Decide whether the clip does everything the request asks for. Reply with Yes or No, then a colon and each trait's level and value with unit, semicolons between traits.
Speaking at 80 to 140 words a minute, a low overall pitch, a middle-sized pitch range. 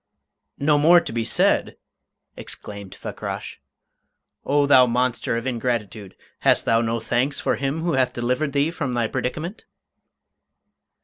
Yes: slow, 135 wpm; low, 125 Hz; average, 3.7 semitones